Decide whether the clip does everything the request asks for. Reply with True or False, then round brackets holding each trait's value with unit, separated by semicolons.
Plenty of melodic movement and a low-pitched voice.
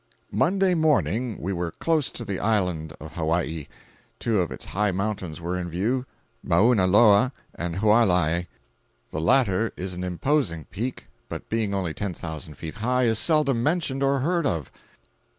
True (6.3 semitones; 100 Hz)